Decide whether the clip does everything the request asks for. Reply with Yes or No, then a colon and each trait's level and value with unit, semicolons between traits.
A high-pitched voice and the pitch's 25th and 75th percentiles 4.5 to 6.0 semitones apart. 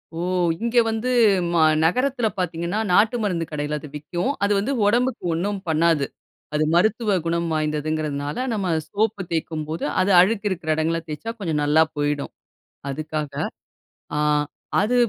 No: medium, 170 Hz; average, 5.1 semitones